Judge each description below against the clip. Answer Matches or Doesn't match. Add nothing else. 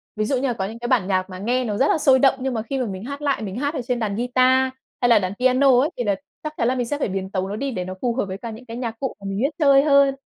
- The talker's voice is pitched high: Matches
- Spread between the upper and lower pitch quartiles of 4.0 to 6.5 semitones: Matches